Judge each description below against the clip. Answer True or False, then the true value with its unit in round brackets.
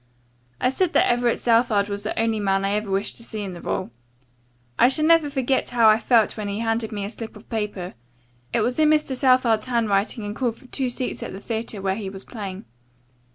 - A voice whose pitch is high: True (225 Hz)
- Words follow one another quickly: True (230 wpm)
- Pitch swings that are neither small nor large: True (3.4 semitones)